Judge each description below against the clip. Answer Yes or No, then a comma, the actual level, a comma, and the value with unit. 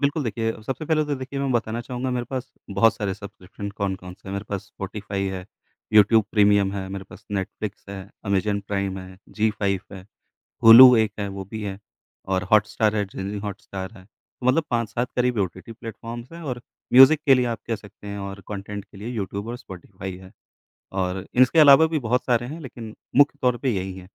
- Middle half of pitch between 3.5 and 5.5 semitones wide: Yes, average, 4.0 semitones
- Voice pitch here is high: No, low, 105 Hz